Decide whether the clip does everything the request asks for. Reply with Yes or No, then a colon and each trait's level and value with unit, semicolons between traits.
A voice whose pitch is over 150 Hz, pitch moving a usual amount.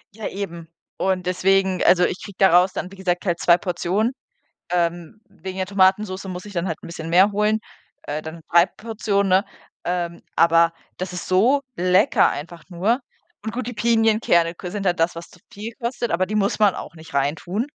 Yes: medium, 185 Hz; average, 3.2 semitones